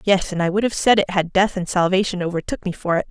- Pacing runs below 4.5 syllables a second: No, 6.5 syllables/s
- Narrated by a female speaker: Yes, female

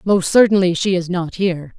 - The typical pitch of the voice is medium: Yes, medium, 180 Hz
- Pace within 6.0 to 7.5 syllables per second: No, 5.4 syllables/s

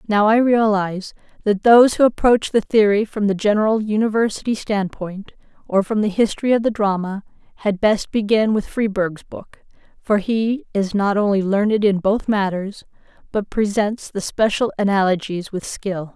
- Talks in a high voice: Yes, high, 205 Hz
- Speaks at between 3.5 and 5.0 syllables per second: Yes, 4.9 syllables/s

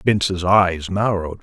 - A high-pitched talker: No, very low, 95 Hz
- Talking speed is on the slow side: Yes, slow, 125 wpm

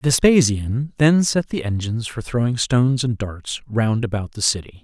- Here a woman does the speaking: No, male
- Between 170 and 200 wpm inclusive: Yes, average, 175 wpm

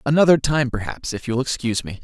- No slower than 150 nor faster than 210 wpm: Yes, fast, 205 wpm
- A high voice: No, low, 125 Hz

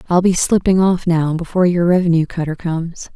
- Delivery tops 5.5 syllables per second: Yes, 5.7 syllables/s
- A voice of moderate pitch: Yes, medium, 170 Hz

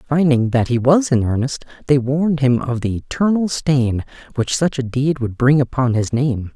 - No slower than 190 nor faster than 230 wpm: Yes, average, 200 wpm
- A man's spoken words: Yes, male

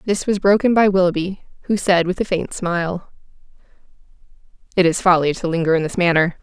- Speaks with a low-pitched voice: No, medium, 180 Hz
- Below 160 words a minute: No, average, 175 wpm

